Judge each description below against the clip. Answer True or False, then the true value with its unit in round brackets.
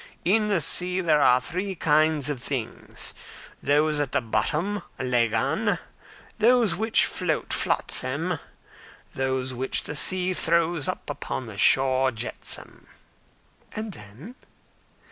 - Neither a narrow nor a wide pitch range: False (5.8 semitones)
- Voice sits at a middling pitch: True (155 Hz)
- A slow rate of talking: True (120 wpm)